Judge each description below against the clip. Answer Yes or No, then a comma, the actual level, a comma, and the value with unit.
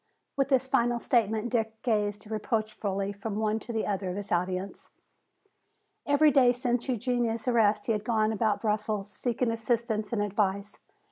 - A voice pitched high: Yes, high, 220 Hz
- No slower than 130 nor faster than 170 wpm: Yes, average, 155 wpm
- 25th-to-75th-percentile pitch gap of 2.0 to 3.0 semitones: Yes, narrow, 2.6 semitones